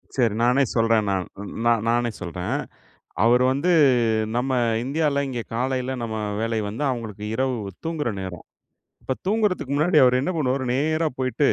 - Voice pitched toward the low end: Yes, low, 125 Hz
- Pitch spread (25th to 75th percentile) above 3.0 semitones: Yes, average, 3.6 semitones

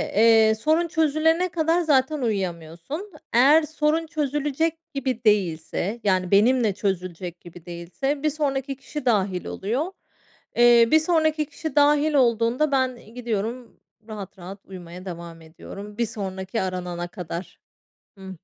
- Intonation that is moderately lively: No, wide, 7.9 semitones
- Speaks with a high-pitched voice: Yes, high, 235 Hz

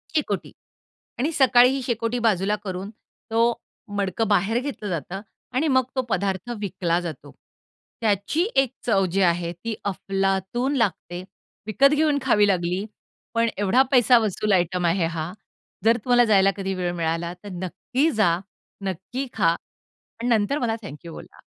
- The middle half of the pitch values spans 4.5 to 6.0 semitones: Yes, average, 4.9 semitones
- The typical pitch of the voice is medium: No, high, 205 Hz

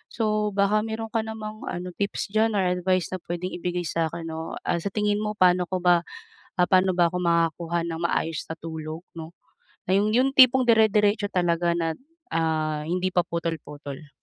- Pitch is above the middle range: No, medium, 180 Hz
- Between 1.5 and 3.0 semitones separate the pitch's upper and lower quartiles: No, average, 4.1 semitones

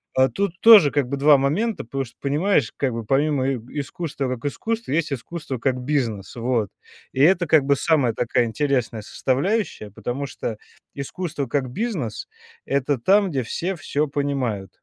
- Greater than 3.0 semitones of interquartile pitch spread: Yes, average, 4.2 semitones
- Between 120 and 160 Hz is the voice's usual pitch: Yes, medium, 140 Hz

